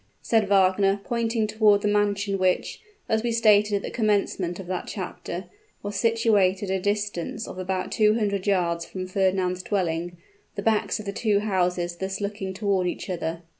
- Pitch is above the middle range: Yes, high, 200 Hz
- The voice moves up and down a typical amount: No, narrow, 2.3 semitones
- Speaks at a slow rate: No, average, 175 wpm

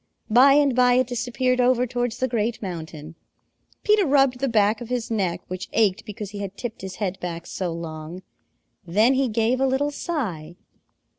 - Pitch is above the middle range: Yes, high, 225 Hz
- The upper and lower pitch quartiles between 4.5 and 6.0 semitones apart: Yes, wide, 5.4 semitones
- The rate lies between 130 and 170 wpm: No, average, 180 wpm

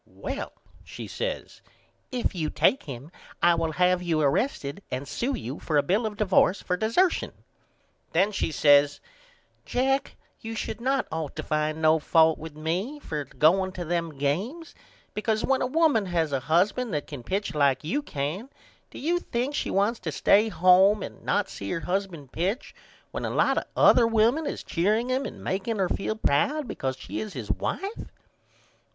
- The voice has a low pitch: No, medium, 185 Hz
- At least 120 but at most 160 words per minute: No, average, 180 wpm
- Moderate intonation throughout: No, wide, 6.7 semitones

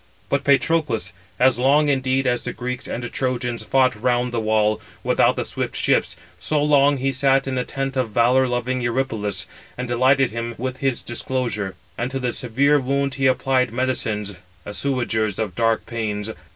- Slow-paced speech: No, average, 170 wpm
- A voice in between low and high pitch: No, low, 125 Hz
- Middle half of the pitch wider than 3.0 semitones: No, narrow, 2.5 semitones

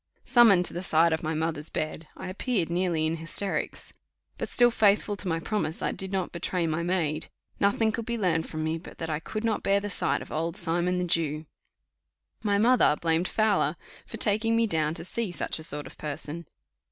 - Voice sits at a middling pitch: Yes, medium, 175 Hz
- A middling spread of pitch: Yes, average, 4.2 semitones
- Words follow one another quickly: Yes, fast, 215 wpm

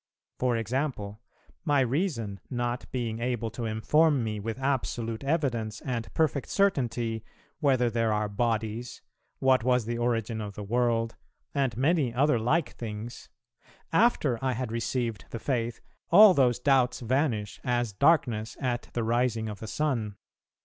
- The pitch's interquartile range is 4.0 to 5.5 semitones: No, average, 2.9 semitones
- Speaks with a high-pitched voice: No, low, 120 Hz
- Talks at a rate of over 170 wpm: No, average, 145 wpm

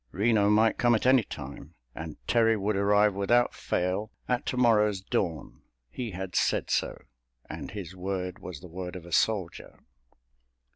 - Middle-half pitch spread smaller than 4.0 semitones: Yes, average, 3.6 semitones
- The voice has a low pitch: Yes, low, 100 Hz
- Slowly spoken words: No, average, 150 wpm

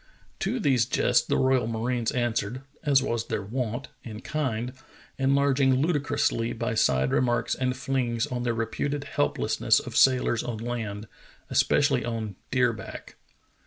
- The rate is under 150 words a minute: Yes, average, 140 wpm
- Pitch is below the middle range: Yes, low, 120 Hz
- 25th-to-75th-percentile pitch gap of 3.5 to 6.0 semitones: No, average, 2.7 semitones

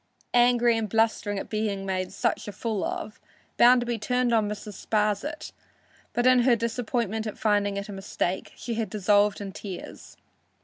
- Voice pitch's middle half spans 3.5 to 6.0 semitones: No, average, 2.7 semitones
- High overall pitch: Yes, high, 215 Hz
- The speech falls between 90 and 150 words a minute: No, average, 165 wpm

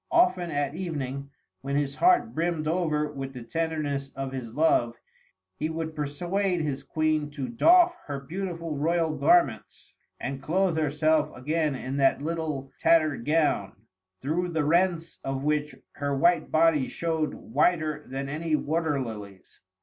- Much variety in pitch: No, average, 3.2 semitones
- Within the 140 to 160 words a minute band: Yes, average, 145 wpm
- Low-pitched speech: No, medium, 155 Hz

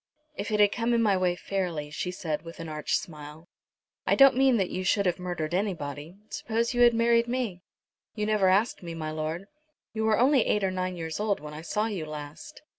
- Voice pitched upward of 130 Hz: Yes, medium, 185 Hz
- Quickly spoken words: Yes, fast, 220 wpm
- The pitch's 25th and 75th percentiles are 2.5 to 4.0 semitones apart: No, wide, 5.4 semitones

